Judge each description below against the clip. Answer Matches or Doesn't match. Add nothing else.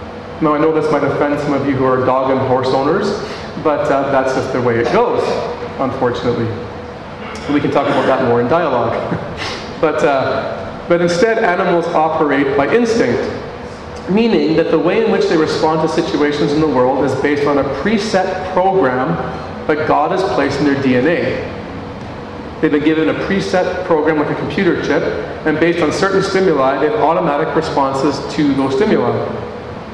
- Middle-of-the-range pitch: Matches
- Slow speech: Doesn't match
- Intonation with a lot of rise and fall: Doesn't match